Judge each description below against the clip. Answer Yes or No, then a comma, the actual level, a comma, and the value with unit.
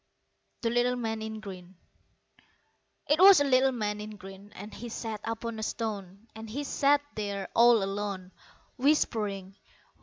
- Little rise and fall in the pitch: No, average, 3.2 semitones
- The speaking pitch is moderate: No, high, 220 Hz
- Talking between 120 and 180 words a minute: Yes, average, 145 wpm